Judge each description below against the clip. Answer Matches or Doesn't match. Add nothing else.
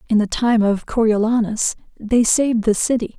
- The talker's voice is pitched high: Matches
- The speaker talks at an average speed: Matches